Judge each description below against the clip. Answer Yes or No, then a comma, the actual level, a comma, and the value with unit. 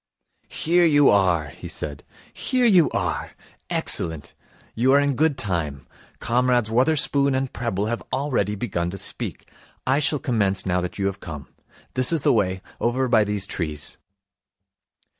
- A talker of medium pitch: No, low, 115 Hz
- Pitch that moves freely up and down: Yes, wide, 6.7 semitones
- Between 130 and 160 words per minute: Yes, average, 155 wpm